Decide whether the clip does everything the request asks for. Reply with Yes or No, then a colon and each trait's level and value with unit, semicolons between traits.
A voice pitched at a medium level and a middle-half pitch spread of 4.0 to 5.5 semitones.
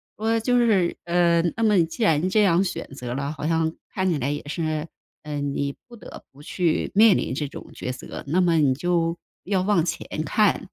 Yes: medium, 170 Hz; average, 4.7 semitones